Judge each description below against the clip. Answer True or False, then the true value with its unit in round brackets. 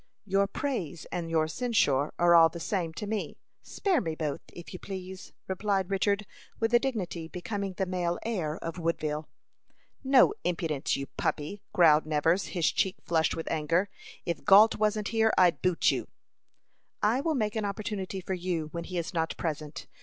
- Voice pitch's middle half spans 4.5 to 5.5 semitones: False (4.0 semitones)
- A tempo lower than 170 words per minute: False (175 wpm)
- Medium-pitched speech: True (180 Hz)